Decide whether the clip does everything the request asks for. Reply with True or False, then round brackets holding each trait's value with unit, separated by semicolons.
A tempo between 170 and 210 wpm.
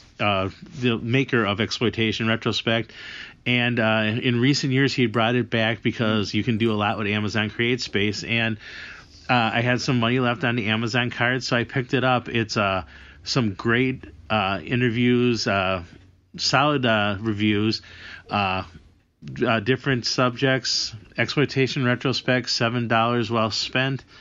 False (150 wpm)